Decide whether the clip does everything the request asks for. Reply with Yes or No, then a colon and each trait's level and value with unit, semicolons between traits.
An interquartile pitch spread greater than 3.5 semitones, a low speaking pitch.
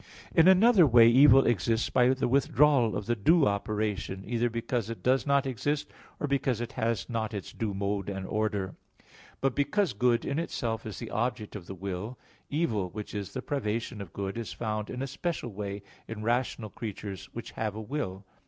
Yes: average, 4.2 semitones; low, 115 Hz